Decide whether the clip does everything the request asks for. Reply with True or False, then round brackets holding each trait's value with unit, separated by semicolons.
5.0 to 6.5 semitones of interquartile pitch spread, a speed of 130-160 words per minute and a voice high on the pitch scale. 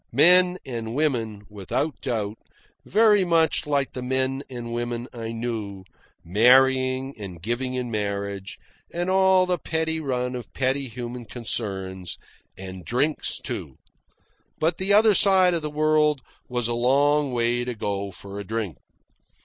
False (5.3 semitones; 145 wpm; 125 Hz)